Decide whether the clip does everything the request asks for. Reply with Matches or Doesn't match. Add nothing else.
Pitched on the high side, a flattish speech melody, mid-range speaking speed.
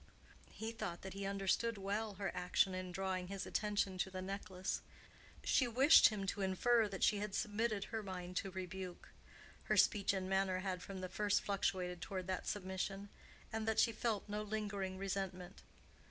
Matches